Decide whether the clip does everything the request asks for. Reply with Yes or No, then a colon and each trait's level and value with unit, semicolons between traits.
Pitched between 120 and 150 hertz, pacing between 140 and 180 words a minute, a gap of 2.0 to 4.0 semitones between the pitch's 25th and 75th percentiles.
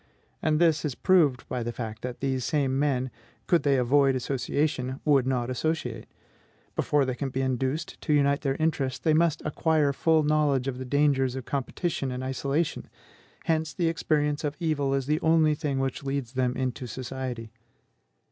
Yes: medium, 140 Hz; average, 175 wpm; average, 2.9 semitones